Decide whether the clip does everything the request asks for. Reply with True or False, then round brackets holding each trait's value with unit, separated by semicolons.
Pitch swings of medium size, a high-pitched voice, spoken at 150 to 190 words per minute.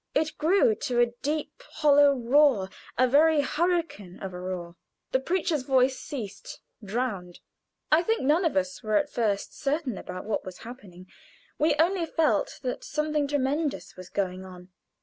False (7.5 semitones; 265 Hz; 160 wpm)